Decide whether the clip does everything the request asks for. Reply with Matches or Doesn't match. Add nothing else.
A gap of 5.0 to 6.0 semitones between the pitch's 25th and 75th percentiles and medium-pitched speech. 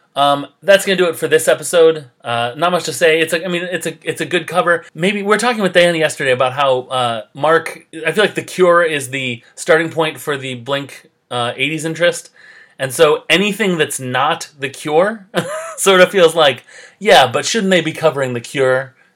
Doesn't match